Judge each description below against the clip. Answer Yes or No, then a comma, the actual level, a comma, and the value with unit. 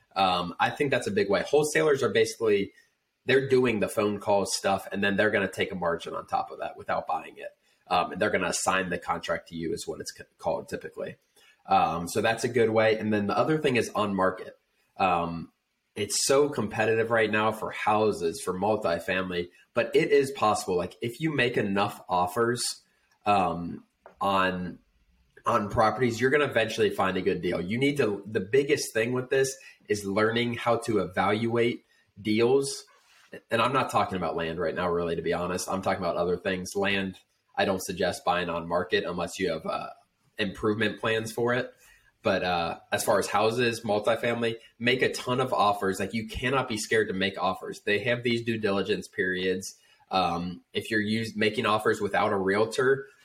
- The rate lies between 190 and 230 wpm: Yes, average, 195 wpm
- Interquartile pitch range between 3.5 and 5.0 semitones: Yes, average, 3.9 semitones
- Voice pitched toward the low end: Yes, low, 110 Hz